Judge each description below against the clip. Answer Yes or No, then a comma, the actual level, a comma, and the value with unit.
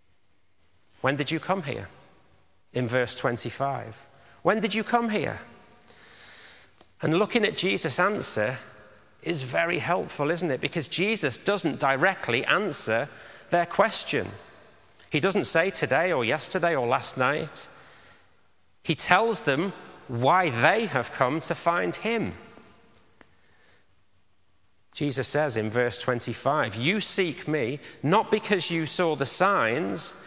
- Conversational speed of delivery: No, slow, 125 wpm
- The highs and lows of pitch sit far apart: Yes, wide, 7.4 semitones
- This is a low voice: No, medium, 145 Hz